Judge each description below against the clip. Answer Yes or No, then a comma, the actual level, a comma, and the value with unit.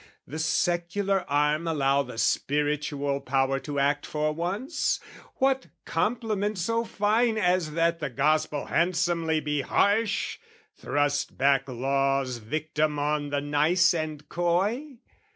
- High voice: No, medium, 155 Hz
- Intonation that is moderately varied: Yes, average, 4.2 semitones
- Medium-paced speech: No, slow, 120 wpm